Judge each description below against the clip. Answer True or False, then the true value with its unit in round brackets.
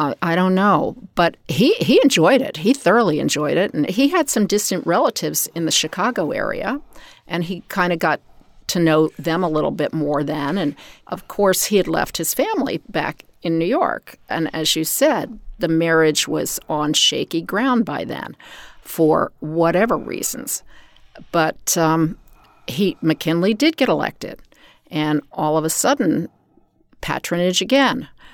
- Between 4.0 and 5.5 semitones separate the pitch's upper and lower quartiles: True (4.4 semitones)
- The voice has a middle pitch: True (170 Hz)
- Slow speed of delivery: False (165 wpm)